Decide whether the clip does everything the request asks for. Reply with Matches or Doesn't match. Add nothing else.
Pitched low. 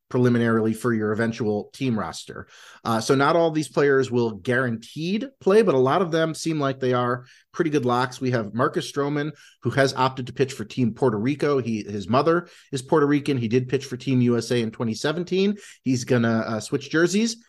Matches